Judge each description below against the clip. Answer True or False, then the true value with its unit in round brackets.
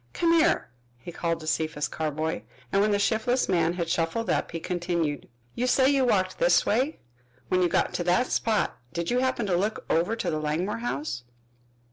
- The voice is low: False (180 Hz)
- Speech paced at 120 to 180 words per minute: False (195 wpm)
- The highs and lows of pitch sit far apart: True (6.0 semitones)